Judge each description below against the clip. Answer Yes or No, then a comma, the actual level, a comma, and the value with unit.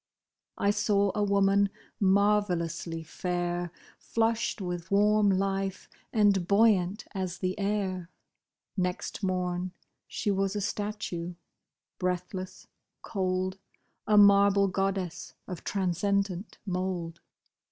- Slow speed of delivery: Yes, slow, 100 wpm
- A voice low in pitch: No, high, 195 Hz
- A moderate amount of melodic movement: No, narrow, 1.9 semitones